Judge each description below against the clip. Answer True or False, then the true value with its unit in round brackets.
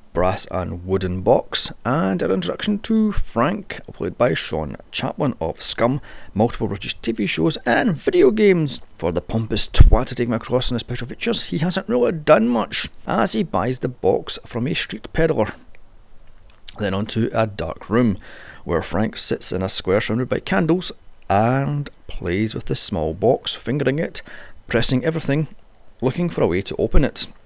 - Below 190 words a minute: True (175 wpm)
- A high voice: False (120 Hz)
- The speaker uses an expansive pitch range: True (7.7 semitones)